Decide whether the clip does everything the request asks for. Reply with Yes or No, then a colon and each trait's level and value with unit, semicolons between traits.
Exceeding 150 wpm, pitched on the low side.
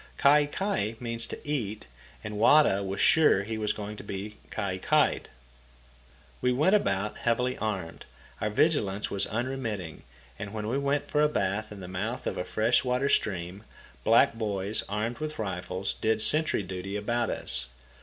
Yes: average, 165 wpm; low, 110 Hz